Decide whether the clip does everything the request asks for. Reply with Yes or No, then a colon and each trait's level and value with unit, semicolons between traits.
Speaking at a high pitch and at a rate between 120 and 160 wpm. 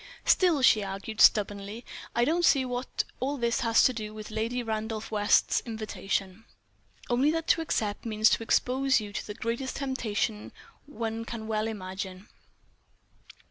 Yes: high, 225 Hz; average, 150 wpm